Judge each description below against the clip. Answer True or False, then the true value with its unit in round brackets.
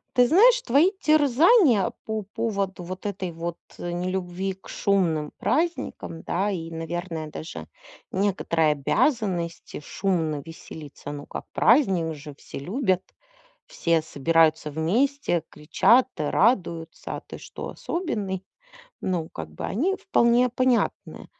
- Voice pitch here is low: False (185 Hz)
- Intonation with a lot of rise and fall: True (6.4 semitones)